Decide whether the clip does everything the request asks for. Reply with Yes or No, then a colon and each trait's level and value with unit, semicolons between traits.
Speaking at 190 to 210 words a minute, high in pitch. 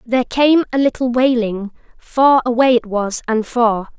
No: average, 165 wpm; high, 240 Hz